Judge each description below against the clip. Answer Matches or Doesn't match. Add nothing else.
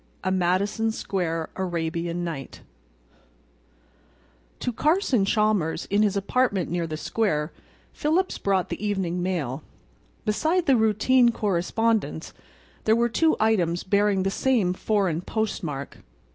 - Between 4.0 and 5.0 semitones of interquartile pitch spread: Matches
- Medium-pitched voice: Doesn't match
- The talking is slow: Matches